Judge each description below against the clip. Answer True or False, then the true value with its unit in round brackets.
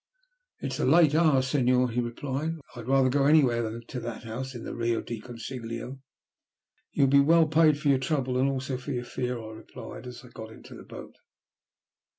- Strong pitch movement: False (2.9 semitones)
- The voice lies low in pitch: True (130 Hz)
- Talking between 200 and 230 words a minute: True (205 wpm)